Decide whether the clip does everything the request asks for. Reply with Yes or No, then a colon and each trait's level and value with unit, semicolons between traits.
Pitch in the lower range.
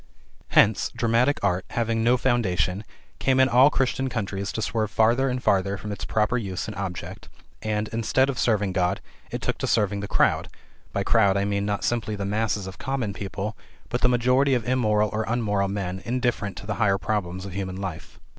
Yes: low, 105 Hz